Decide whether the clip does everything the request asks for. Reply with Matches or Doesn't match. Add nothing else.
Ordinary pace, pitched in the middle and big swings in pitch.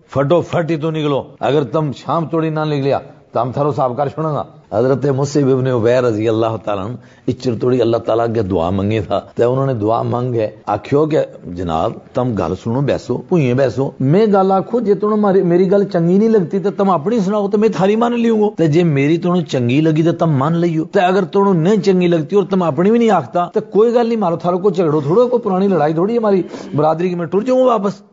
Doesn't match